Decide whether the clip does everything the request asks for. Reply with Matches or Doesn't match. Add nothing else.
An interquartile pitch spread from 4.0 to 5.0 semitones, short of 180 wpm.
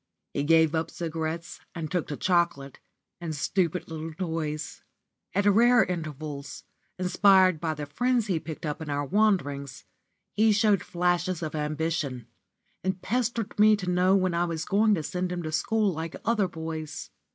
Doesn't match